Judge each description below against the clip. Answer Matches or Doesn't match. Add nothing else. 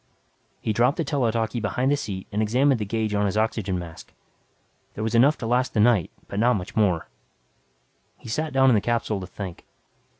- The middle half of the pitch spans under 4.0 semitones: Matches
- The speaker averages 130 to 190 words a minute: Doesn't match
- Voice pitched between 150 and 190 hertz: Doesn't match